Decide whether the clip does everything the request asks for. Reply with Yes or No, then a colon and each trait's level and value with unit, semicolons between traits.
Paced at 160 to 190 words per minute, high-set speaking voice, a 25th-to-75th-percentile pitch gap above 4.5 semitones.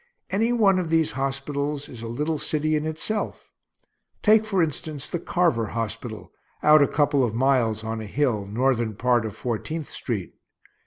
No: average, 165 wpm; medium, 140 Hz; wide, 5.4 semitones